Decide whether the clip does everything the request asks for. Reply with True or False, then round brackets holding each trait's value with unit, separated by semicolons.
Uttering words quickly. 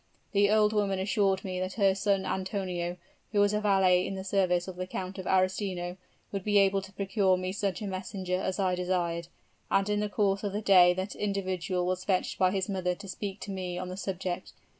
True (220 wpm)